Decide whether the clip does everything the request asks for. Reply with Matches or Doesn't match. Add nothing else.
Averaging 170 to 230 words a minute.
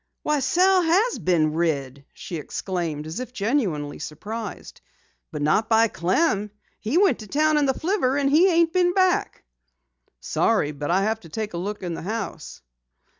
Matches